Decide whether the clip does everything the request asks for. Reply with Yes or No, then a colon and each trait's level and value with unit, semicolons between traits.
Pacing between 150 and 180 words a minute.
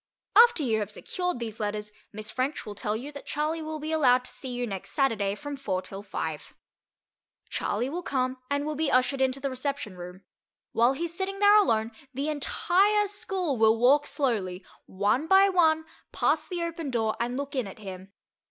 No: average, 195 wpm